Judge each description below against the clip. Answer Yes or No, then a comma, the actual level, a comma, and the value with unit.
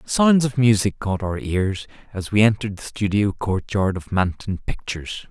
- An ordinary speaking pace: Yes, average, 170 wpm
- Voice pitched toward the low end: Yes, low, 105 Hz